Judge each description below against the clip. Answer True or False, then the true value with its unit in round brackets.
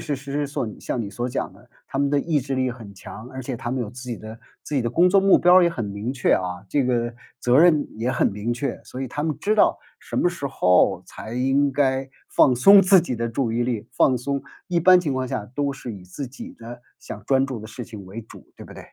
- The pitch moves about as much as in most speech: True (3.5 semitones)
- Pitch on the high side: False (130 Hz)